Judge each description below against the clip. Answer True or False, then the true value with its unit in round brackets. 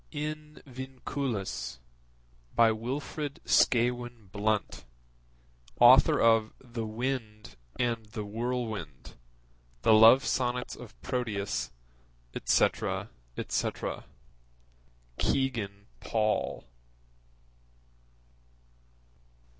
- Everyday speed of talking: False (65 wpm)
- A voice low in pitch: True (115 Hz)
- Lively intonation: False (2.8 semitones)